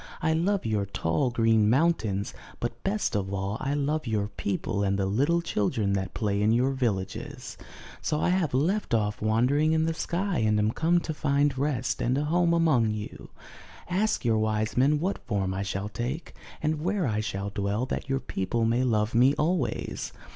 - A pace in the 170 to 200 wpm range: Yes, average, 190 wpm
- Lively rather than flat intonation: Yes, wide, 6.7 semitones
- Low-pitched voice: Yes, low, 120 Hz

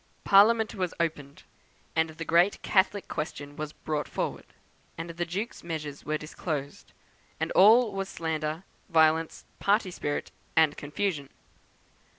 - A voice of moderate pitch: Yes, medium, 165 Hz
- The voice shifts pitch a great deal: No, average, 4.1 semitones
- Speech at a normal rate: No, slow, 130 wpm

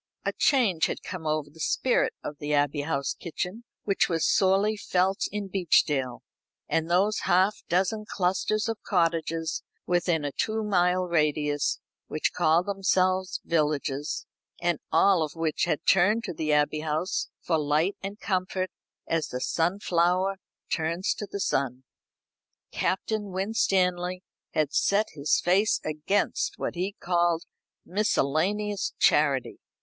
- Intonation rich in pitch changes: No, average, 4.0 semitones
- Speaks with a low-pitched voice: No, medium, 175 Hz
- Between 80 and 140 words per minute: Yes, slow, 135 wpm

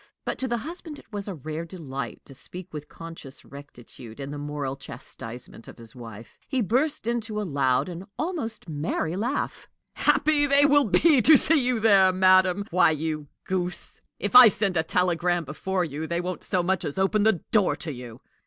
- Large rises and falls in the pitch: Yes, wide, 6.9 semitones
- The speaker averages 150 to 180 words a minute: No, average, 190 wpm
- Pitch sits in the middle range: Yes, medium, 180 Hz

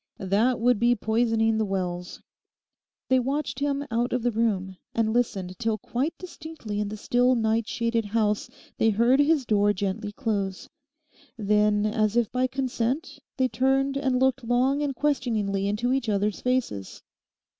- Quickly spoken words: No, average, 155 wpm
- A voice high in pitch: Yes, high, 230 Hz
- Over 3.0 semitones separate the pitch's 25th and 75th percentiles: Yes, average, 3.6 semitones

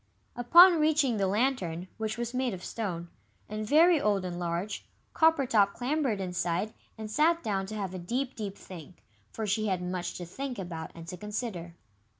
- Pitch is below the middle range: No, high, 210 Hz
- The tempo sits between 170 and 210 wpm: Yes, average, 175 wpm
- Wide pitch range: Yes, wide, 5.8 semitones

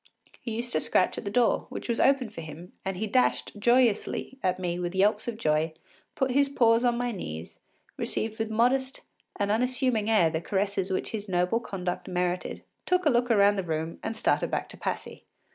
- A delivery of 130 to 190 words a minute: No, average, 200 wpm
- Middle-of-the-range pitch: No, high, 210 Hz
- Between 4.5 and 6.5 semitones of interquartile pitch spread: Yes, average, 5.1 semitones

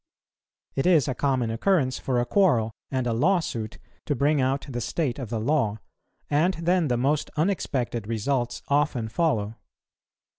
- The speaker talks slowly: No, average, 155 wpm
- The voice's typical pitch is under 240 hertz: Yes, low, 135 Hz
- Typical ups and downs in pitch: Yes, average, 4.6 semitones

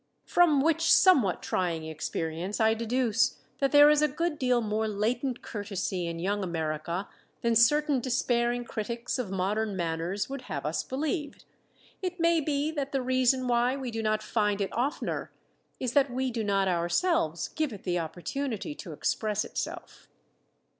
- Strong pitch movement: Yes, wide, 6.1 semitones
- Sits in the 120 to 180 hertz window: No, high, 235 Hz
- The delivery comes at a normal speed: Yes, average, 160 wpm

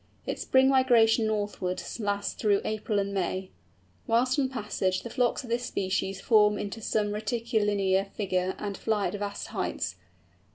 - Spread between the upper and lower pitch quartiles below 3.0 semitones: Yes, narrow, 2.6 semitones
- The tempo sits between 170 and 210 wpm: No, average, 155 wpm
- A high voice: Yes, high, 210 Hz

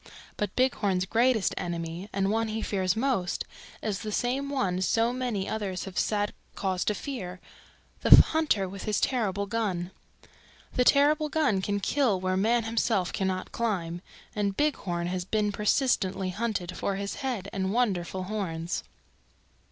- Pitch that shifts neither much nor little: Yes, average, 3.9 semitones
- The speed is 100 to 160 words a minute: Yes, average, 150 wpm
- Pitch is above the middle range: Yes, high, 200 Hz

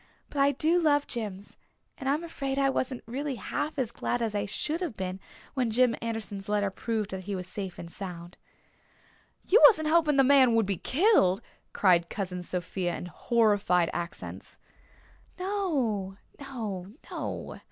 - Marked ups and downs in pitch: Yes, wide, 6.6 semitones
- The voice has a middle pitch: No, high, 225 Hz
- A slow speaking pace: No, average, 160 wpm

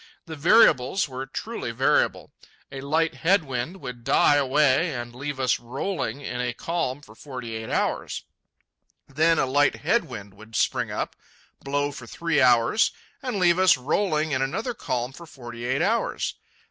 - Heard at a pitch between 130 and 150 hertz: Yes, medium, 140 Hz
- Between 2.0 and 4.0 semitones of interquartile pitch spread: No, average, 4.7 semitones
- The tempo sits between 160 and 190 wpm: Yes, average, 165 wpm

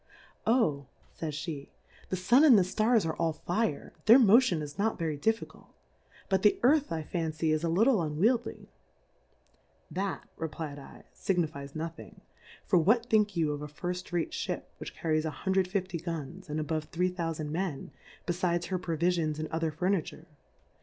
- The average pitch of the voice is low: No, medium, 170 Hz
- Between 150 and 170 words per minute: Yes, average, 165 wpm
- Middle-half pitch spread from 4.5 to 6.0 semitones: No, average, 3.8 semitones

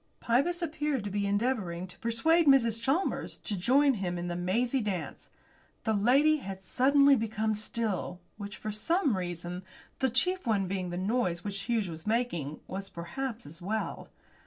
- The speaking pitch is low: No, high, 215 Hz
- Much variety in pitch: Yes, wide, 6.0 semitones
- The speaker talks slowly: No, average, 165 wpm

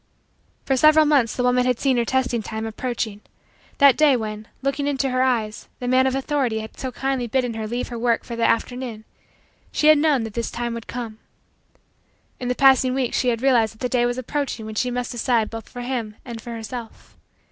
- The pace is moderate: No, fast, 215 wpm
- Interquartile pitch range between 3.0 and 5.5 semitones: No, narrow, 2.4 semitones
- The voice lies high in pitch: Yes, high, 245 Hz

